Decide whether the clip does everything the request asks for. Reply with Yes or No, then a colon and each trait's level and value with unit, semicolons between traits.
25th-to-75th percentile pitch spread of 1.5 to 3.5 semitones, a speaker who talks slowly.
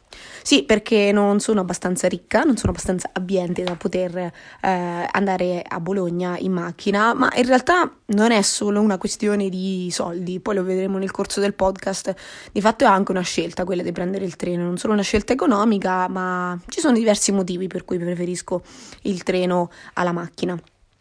No: narrow, 2.5 semitones; fast, 180 wpm